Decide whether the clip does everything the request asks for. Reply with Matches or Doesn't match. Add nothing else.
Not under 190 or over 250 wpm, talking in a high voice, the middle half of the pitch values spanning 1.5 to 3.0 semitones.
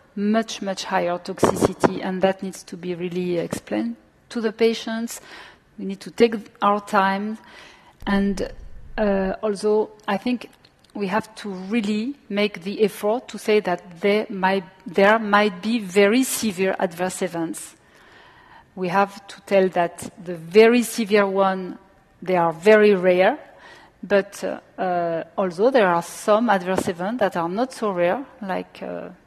Doesn't match